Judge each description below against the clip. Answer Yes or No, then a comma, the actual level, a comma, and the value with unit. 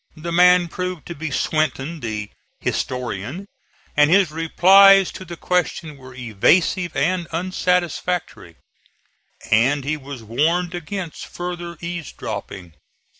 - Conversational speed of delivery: No, slow, 120 wpm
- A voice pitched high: No, medium, 165 Hz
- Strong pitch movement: No, average, 4.5 semitones